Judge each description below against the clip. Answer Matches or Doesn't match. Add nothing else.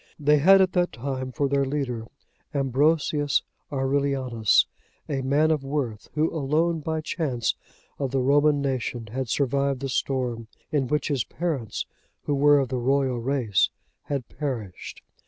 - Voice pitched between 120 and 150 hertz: Matches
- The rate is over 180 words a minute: Doesn't match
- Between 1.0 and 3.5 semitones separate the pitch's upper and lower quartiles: Matches